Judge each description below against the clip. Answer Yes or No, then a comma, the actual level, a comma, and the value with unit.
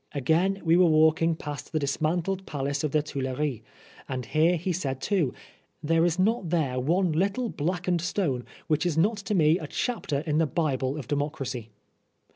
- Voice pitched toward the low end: No, medium, 160 Hz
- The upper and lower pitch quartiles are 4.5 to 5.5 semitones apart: No, average, 3.9 semitones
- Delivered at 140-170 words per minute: No, average, 185 wpm